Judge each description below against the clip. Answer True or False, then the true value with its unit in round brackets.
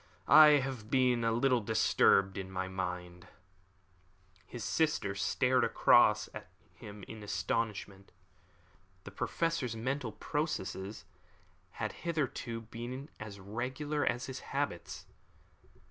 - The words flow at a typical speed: False (110 wpm)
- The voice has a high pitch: False (115 Hz)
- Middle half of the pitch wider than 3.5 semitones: True (4.5 semitones)